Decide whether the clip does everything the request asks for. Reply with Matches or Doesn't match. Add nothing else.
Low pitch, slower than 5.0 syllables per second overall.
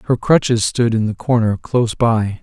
Matches